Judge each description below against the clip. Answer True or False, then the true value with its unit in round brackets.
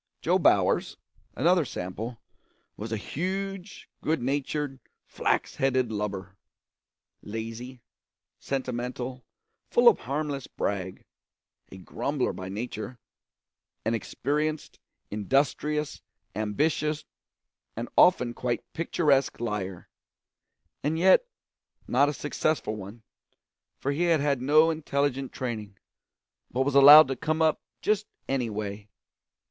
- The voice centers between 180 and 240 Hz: False (130 Hz)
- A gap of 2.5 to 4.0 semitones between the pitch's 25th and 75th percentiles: False (5.3 semitones)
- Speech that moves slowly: True (110 wpm)